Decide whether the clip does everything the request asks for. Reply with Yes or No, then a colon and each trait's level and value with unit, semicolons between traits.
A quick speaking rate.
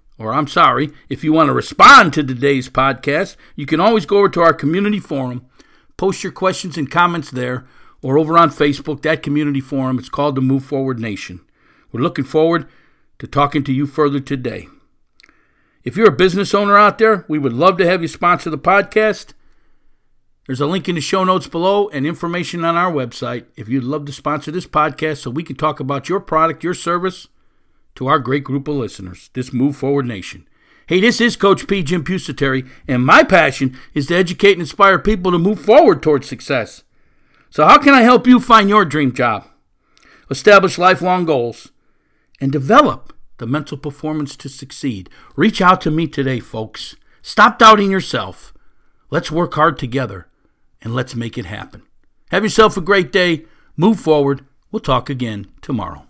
No: average, 185 wpm